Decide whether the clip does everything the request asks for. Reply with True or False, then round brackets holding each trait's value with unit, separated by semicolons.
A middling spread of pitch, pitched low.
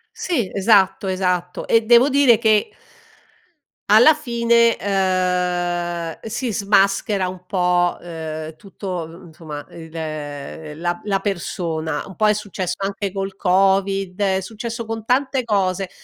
False (3.4 semitones; 195 Hz)